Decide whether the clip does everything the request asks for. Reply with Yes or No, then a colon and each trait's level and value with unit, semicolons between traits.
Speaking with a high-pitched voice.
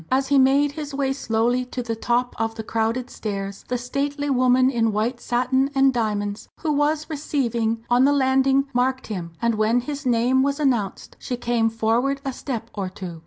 Yes: very high, 250 Hz